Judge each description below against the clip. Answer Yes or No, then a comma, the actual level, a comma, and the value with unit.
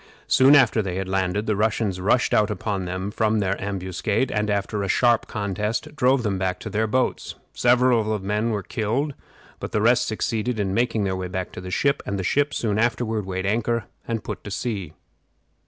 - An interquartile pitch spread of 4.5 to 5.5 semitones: No, average, 3.3 semitones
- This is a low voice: Yes, low, 105 Hz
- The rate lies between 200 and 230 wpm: Yes, fast, 205 wpm